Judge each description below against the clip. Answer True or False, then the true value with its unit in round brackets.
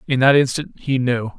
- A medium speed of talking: False (215 wpm)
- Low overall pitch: True (130 Hz)